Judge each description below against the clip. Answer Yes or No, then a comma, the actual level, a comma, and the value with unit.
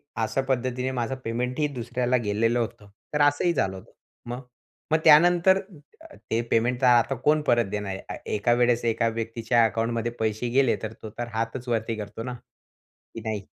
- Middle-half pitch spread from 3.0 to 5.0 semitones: No, narrow, 2.6 semitones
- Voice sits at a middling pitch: No, low, 120 Hz